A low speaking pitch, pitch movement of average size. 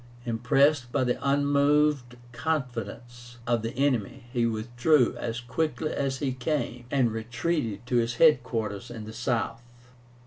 Yes: low, 120 Hz; average, 3.3 semitones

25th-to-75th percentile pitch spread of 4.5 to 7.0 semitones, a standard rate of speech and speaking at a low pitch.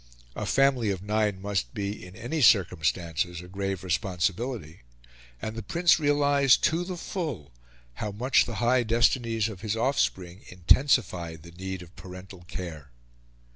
Yes: wide, 5.5 semitones; average, 145 wpm; low, 100 Hz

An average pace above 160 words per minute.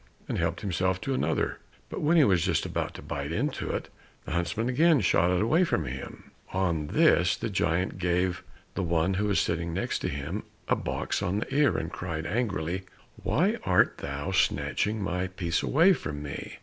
Yes: average, 190 wpm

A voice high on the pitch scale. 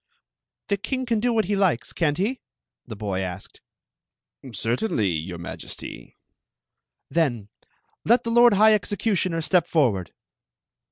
No: medium, 170 Hz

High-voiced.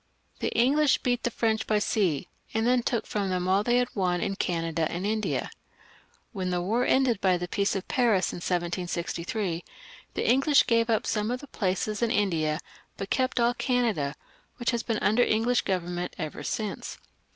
Yes: high, 210 Hz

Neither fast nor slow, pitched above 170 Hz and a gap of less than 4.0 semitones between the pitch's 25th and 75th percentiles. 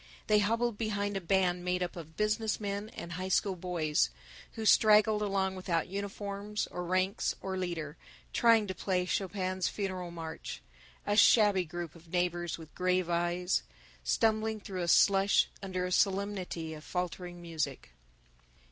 Yes: average, 150 wpm; medium, 185 Hz; average, 2.7 semitones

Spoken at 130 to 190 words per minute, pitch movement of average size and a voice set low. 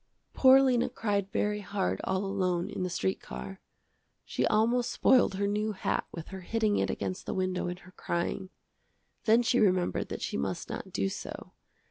No: average, 180 wpm; average, 3.0 semitones; high, 195 Hz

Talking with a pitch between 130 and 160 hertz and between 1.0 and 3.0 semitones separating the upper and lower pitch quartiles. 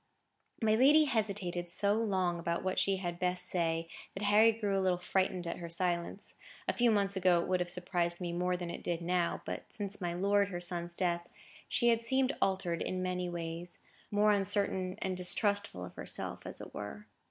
No: medium, 185 Hz; average, 2.7 semitones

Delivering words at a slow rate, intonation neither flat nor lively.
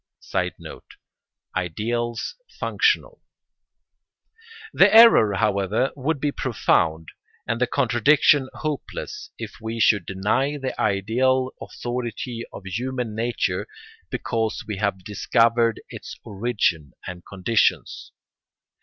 Yes: slow, 100 wpm; average, 4.5 semitones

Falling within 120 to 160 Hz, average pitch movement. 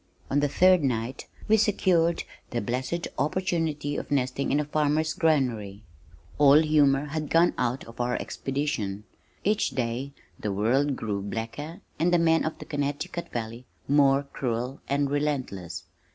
Yes: medium, 140 Hz; average, 4.4 semitones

